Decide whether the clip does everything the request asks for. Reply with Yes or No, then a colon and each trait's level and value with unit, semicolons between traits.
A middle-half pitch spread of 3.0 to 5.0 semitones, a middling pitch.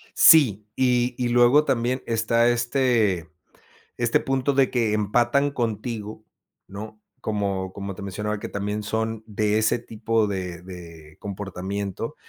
No: average, 3.3 semitones; low, 110 Hz